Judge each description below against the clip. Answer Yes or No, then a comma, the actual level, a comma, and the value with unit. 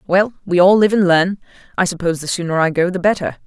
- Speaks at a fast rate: Yes, fast, 240 wpm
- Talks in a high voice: No, medium, 180 Hz